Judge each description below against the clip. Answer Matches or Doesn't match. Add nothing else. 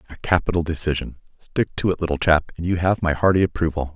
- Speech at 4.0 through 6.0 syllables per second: Doesn't match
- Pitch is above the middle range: Doesn't match